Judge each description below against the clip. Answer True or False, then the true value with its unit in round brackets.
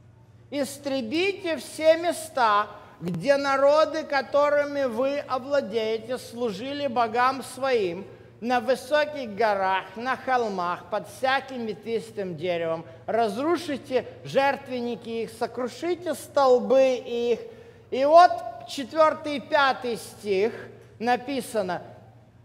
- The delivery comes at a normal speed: False (85 wpm)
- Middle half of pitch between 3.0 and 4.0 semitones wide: False (4.6 semitones)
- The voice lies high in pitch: True (255 Hz)